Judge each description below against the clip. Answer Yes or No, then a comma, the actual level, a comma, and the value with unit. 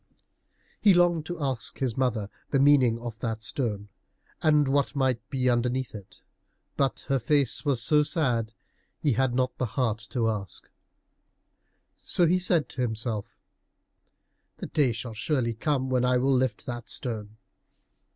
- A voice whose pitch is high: No, low, 125 Hz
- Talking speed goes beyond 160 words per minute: No, average, 155 wpm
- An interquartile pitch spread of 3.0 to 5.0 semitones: Yes, average, 3.6 semitones